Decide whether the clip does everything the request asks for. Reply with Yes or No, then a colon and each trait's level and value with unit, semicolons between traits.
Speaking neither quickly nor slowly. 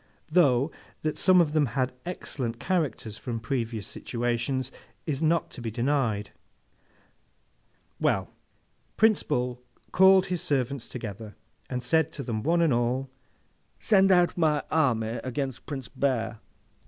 No: slow, 130 wpm